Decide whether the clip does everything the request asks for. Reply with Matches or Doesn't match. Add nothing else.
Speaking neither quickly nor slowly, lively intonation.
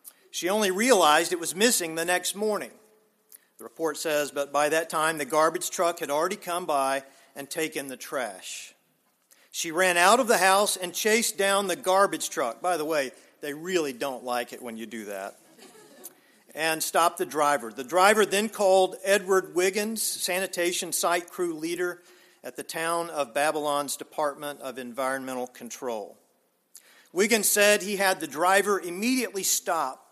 Doesn't match